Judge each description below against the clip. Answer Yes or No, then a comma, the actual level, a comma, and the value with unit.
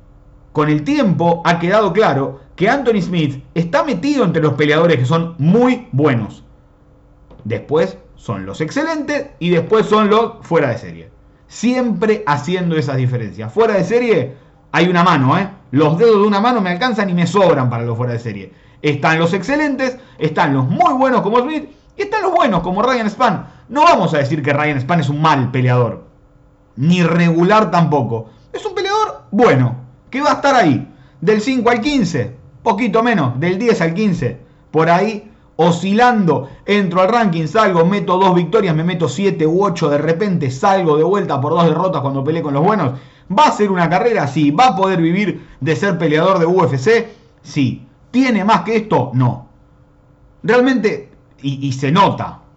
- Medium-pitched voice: Yes, medium, 170 Hz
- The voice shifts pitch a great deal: Yes, wide, 7.2 semitones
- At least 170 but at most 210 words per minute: Yes, average, 180 wpm